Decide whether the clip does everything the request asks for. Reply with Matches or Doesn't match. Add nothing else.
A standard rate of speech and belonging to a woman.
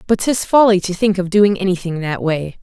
Doesn't match